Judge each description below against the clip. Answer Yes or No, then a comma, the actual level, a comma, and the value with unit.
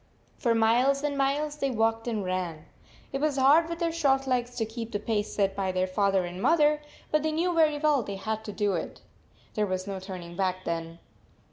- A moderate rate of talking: No, fast, 215 wpm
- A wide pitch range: Yes, wide, 6.7 semitones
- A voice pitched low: No, high, 225 Hz